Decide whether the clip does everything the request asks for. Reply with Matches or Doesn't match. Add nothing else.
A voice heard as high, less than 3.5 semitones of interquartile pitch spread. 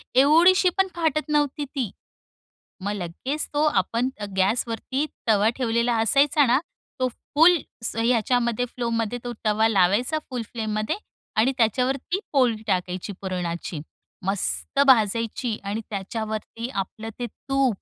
Doesn't match